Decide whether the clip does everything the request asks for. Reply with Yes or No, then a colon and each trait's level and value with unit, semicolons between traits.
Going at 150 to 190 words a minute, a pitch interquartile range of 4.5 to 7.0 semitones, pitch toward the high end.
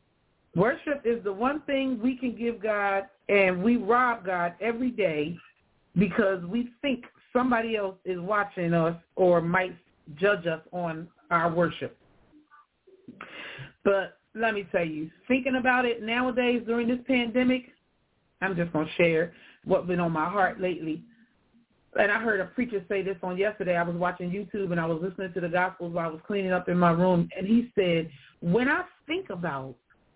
Yes: average, 175 wpm; average, 5.3 semitones; high, 195 Hz